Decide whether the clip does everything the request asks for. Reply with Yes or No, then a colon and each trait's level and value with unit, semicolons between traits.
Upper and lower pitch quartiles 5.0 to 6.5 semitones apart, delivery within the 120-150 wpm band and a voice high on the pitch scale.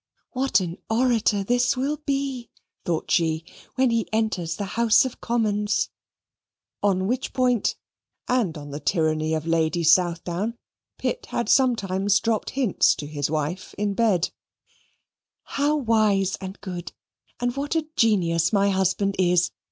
Yes: wide, 5.6 semitones; average, 140 wpm; high, 200 Hz